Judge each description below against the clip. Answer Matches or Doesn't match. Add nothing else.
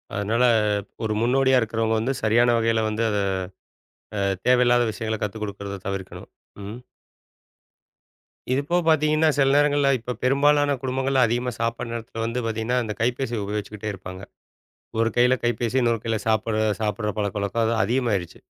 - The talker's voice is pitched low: Matches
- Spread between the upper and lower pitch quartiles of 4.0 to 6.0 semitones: Doesn't match